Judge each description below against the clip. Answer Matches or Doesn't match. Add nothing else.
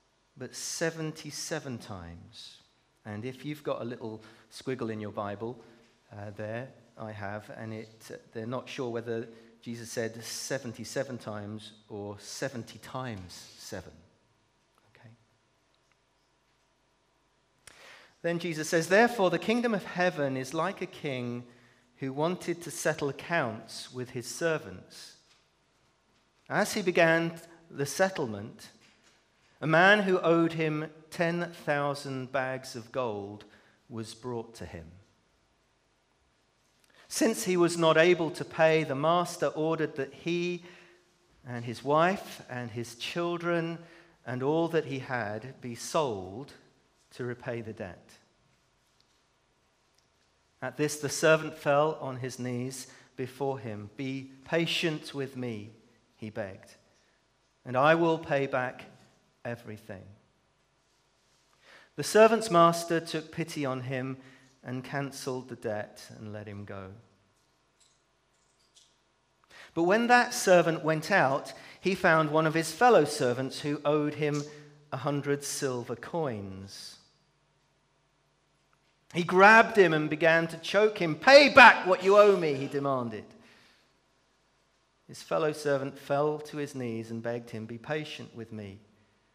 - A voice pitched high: Doesn't match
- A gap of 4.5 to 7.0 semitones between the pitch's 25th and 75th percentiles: Matches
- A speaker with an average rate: Doesn't match